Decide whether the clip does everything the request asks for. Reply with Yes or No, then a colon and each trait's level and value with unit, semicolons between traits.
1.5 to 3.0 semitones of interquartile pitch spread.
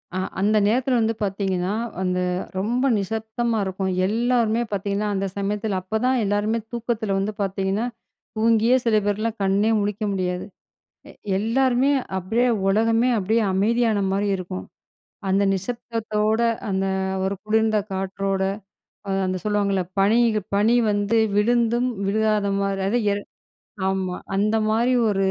Yes: narrow, 2.6 semitones